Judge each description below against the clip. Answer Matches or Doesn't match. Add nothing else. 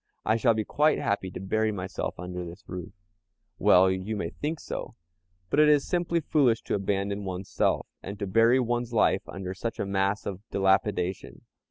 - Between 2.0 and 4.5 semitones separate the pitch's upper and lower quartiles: Matches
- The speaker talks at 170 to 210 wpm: Matches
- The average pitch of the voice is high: Doesn't match